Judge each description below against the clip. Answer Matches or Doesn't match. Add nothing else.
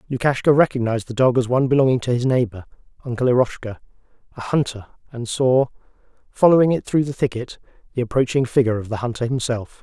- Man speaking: Matches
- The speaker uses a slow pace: Doesn't match